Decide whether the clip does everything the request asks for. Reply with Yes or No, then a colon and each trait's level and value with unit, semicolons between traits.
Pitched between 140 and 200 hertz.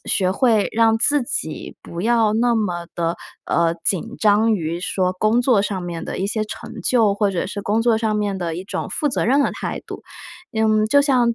No: high, 215 Hz